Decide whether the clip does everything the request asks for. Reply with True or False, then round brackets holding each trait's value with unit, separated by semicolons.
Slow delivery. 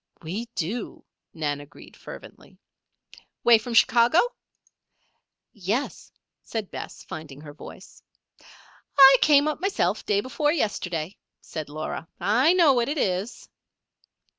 True (115 wpm)